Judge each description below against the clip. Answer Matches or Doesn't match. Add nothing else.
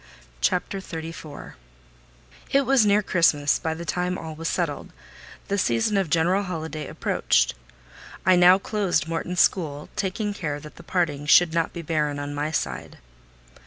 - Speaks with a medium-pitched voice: Matches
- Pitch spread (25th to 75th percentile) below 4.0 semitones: Matches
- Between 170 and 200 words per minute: Doesn't match